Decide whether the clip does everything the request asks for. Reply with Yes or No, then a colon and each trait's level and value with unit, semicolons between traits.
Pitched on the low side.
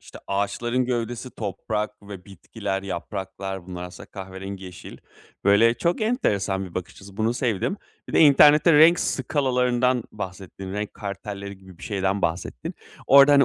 Yes: low, 100 Hz